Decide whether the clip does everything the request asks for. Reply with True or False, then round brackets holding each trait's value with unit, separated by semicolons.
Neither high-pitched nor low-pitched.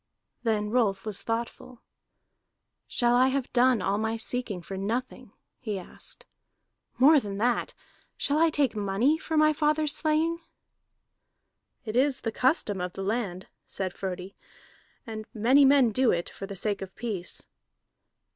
False (230 Hz)